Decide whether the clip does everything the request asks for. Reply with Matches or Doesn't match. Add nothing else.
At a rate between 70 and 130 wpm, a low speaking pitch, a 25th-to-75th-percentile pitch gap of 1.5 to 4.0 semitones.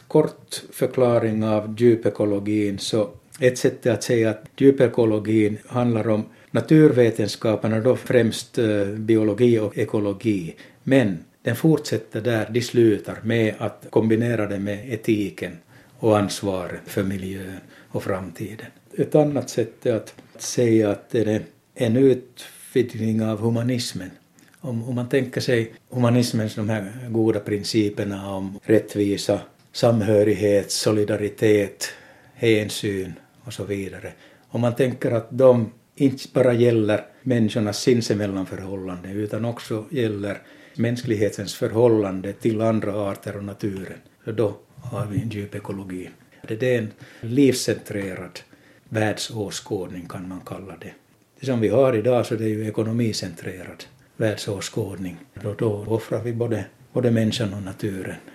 Matches